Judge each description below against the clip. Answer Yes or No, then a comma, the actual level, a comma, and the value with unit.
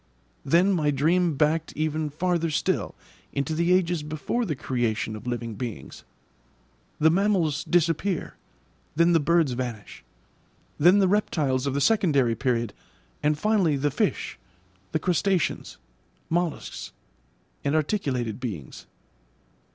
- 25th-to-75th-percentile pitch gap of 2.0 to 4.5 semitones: No, average, 4.9 semitones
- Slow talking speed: Yes, slow, 120 wpm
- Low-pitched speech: No, medium, 155 Hz